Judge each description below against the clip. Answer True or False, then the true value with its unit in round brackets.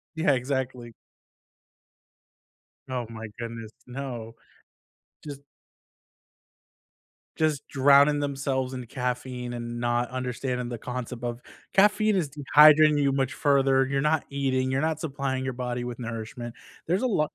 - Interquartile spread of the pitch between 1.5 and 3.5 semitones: True (2.7 semitones)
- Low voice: True (130 Hz)